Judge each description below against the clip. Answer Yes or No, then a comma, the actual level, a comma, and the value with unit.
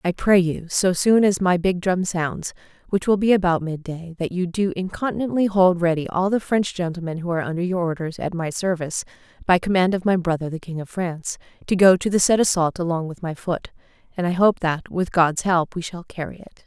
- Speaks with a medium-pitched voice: Yes, medium, 180 Hz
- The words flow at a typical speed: No, fast, 225 wpm